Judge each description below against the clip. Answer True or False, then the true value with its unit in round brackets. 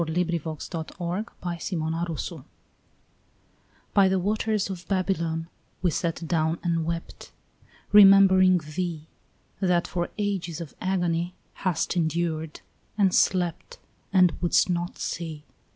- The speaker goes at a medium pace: False (105 wpm)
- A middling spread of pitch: False (2.3 semitones)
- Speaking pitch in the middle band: True (175 Hz)